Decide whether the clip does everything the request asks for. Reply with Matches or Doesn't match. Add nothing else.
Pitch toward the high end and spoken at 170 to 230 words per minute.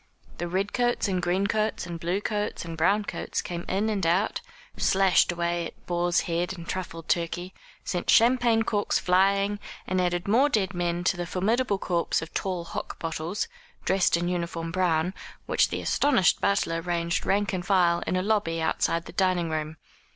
Doesn't match